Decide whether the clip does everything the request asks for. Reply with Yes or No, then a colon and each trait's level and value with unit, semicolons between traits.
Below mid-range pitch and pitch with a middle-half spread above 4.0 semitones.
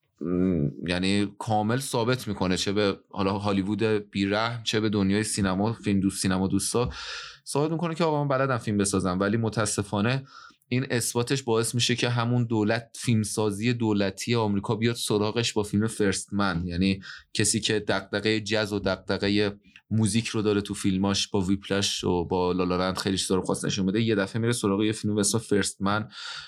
No: low, 105 Hz; narrow, 2.5 semitones